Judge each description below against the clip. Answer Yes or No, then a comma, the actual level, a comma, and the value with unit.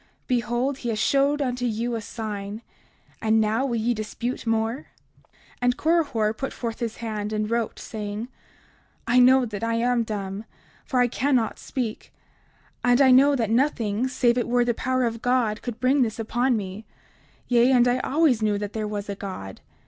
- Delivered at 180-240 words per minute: Yes, average, 185 wpm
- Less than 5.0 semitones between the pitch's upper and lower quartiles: Yes, narrow, 2.6 semitones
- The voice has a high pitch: Yes, high, 235 Hz